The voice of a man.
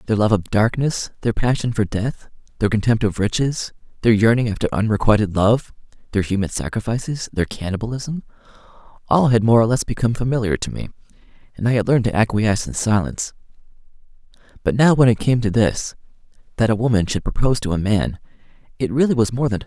Yes: male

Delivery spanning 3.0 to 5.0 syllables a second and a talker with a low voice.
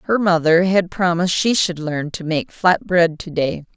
No: 4.6 syllables/s; medium, 170 Hz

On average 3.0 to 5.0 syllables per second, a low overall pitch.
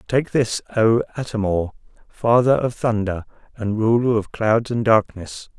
Yes: 4.3 syllables/s; low, 110 Hz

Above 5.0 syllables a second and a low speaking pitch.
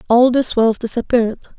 No: 5.7 syllables/s; high, 235 Hz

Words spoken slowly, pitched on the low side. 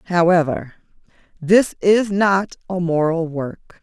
No: slow, 110 wpm; medium, 175 Hz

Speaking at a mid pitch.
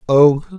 Yes: medium, 155 Hz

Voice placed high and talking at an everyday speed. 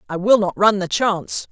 No: high, 200 Hz; fast, 235 wpm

